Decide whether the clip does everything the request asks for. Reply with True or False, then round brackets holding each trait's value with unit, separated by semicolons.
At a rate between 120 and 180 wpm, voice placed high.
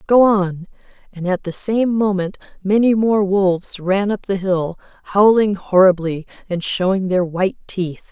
True (155 wpm; 195 Hz)